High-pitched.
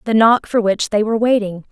Yes: high, 215 Hz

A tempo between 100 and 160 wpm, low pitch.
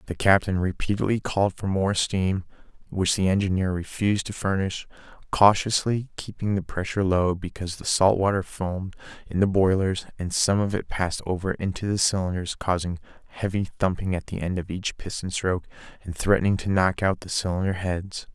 No: average, 175 wpm; very low, 95 Hz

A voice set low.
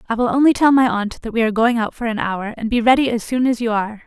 No: high, 230 Hz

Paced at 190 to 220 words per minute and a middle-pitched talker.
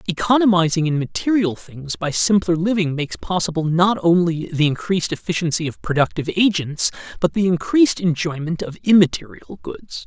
No: average, 145 wpm; medium, 170 Hz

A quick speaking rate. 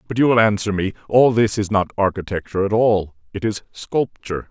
No: average, 185 wpm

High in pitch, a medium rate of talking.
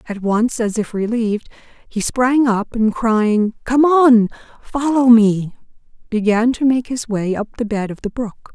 Yes: high, 230 Hz; average, 175 wpm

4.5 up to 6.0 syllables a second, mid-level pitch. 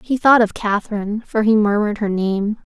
No: 5.5 syllables/s; high, 215 Hz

